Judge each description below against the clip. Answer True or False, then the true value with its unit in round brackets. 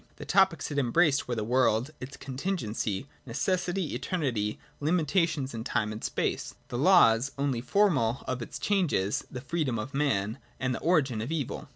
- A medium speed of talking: True (165 wpm)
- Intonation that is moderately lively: False (5.9 semitones)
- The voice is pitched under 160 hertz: True (135 Hz)